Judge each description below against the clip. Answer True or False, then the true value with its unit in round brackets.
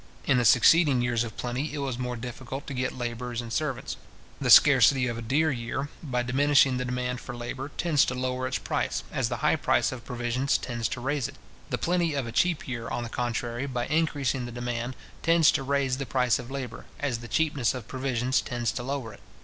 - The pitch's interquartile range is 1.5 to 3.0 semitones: True (2.4 semitones)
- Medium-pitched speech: False (125 Hz)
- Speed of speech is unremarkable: False (220 wpm)